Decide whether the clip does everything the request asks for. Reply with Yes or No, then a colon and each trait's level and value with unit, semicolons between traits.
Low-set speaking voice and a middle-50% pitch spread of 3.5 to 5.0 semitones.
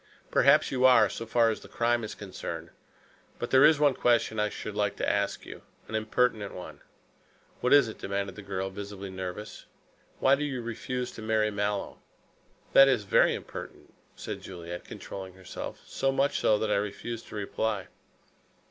Yes: low, 110 Hz; average, 3.9 semitones